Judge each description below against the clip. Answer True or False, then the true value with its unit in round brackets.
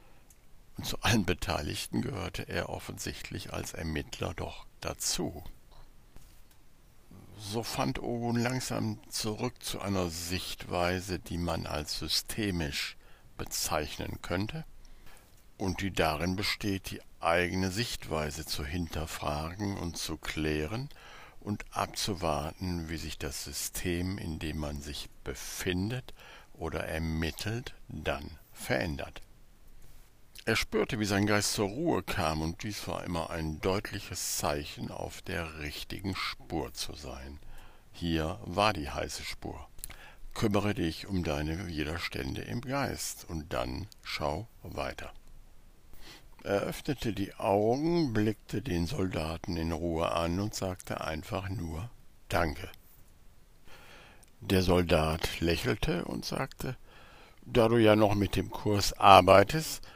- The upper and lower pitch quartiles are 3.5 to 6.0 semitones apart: True (4.6 semitones)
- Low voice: True (90 Hz)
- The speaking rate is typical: False (115 wpm)